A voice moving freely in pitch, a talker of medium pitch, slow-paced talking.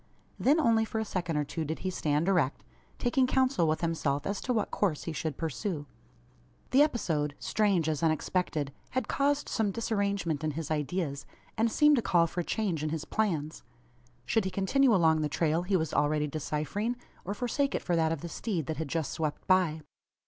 No: wide, 5.8 semitones; medium, 170 Hz; average, 200 wpm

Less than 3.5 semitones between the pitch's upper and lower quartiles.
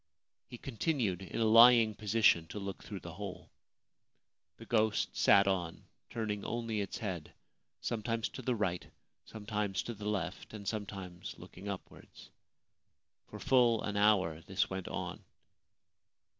Yes: average, 2.9 semitones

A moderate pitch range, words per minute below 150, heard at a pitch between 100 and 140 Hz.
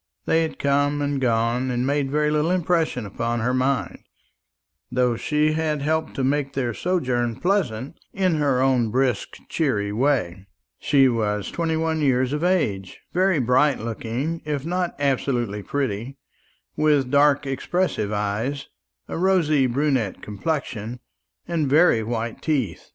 Yes: average, 4.4 semitones; average, 140 wpm; low, 135 Hz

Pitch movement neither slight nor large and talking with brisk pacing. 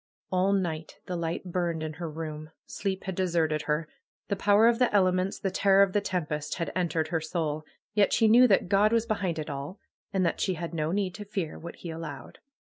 Yes: average, 3.8 semitones; fast, 215 wpm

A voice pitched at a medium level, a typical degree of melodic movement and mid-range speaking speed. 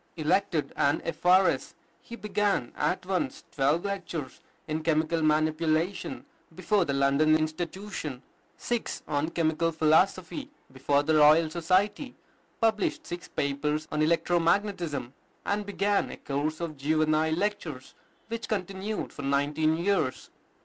No: medium, 160 Hz; average, 4.0 semitones; slow, 120 wpm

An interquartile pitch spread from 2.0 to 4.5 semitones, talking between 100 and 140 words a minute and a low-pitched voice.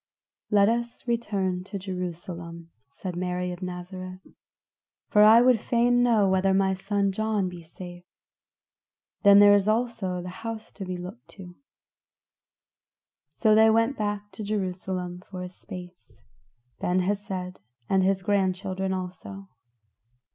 No: narrow, 2.5 semitones; slow, 135 wpm; high, 190 Hz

